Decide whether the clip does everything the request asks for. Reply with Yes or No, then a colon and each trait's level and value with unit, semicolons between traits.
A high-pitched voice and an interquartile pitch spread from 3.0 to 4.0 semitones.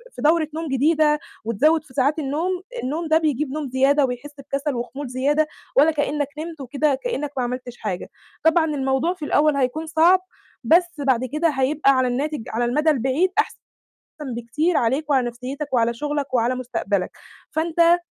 Yes: very high, 290 Hz; average, 3.4 semitones